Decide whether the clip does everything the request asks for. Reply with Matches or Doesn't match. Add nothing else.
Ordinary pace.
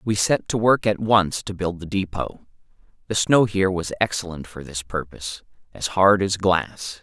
Matches